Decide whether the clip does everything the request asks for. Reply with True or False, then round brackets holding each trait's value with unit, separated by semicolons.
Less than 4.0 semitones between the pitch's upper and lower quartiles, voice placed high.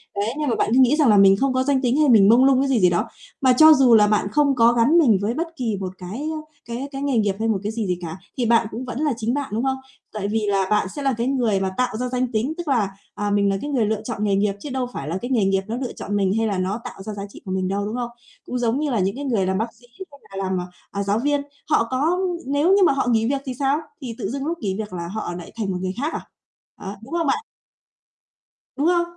False (5.1 semitones; 230 Hz)